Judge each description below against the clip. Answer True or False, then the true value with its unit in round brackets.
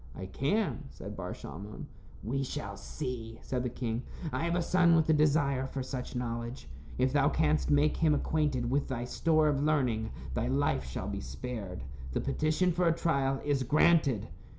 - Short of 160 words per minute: False (180 wpm)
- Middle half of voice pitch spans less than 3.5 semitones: False (4.5 semitones)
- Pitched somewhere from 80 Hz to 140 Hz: True (135 Hz)